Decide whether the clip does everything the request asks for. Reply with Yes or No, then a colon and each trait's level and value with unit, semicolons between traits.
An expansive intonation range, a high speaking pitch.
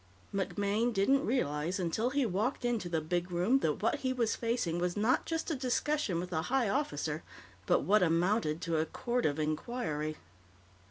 Yes: wide, 6.7 semitones; high, 205 Hz